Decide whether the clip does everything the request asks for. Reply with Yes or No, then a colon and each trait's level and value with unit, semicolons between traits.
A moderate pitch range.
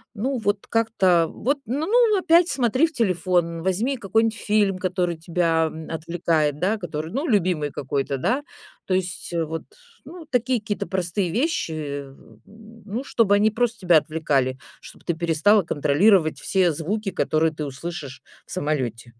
No: wide, 5.8 semitones